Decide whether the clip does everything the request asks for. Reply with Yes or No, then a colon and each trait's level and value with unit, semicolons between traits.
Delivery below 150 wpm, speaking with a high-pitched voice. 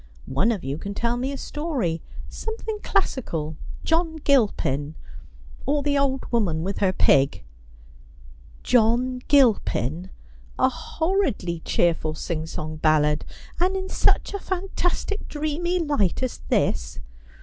Yes: slow, 135 wpm; high, 235 Hz